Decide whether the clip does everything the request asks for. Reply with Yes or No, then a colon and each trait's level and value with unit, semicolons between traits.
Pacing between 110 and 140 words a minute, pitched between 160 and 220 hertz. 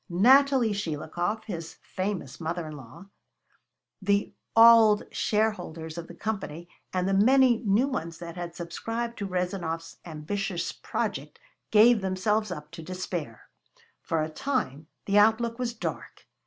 Yes: slow, 135 wpm; high, 190 Hz